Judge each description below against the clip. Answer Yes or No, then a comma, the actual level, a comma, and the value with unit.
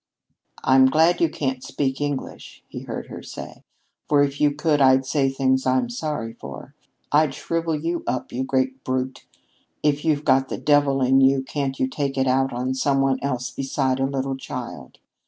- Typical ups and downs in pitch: No, narrow, 1.8 semitones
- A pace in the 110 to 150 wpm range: No, average, 190 wpm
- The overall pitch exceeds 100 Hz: Yes, low, 135 Hz